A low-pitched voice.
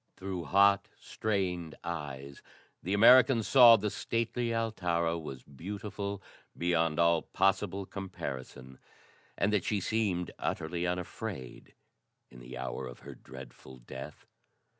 Yes: very low, 90 Hz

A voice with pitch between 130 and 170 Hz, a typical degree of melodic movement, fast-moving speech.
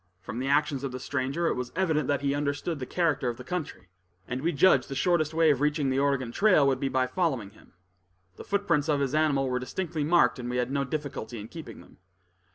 Yes: medium, 140 Hz; average, 3.5 semitones; fast, 230 wpm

